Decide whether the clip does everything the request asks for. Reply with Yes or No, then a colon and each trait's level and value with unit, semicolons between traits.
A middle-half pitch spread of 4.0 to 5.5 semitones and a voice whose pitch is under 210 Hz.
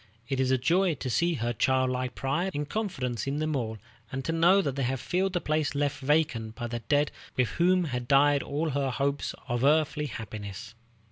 No: average, 3.6 semitones; medium, 140 Hz